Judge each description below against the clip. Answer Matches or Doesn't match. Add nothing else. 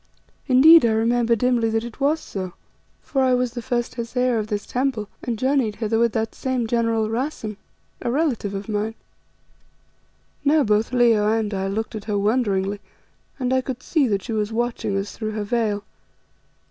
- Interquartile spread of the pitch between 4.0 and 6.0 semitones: Doesn't match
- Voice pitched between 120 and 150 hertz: Doesn't match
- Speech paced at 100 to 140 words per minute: Doesn't match